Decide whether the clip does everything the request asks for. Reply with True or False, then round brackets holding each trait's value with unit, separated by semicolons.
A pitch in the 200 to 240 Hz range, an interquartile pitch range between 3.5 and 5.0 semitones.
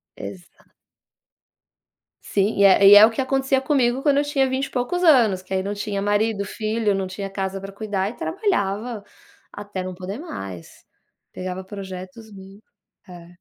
True (205 Hz; 4.3 semitones)